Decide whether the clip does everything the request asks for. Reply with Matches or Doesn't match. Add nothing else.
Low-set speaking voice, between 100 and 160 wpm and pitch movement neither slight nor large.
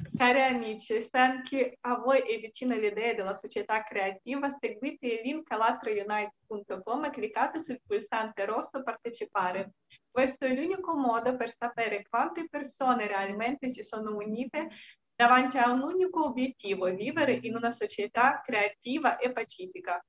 Doesn't match